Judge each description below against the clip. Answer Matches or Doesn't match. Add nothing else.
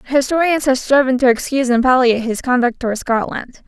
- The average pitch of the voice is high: Matches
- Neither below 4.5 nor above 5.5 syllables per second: Doesn't match